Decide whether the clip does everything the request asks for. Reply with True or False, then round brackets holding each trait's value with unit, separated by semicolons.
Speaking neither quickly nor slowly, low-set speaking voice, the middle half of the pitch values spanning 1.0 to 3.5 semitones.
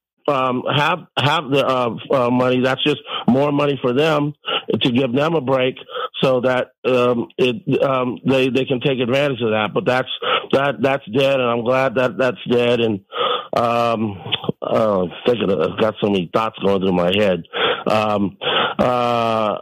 True (175 wpm; 125 Hz; 2.9 semitones)